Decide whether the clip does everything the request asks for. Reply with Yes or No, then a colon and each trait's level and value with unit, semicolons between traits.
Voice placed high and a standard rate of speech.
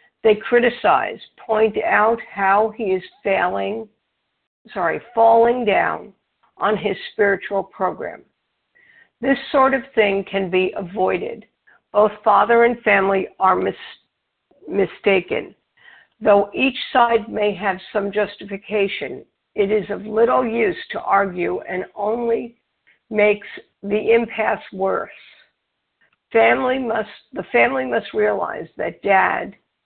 No: high, 215 Hz; slow, 115 wpm